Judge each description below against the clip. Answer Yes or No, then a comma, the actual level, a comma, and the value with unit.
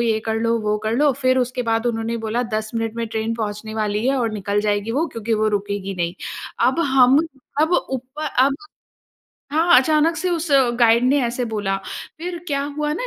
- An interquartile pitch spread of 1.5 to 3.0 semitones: No, average, 4.0 semitones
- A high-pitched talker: Yes, high, 230 Hz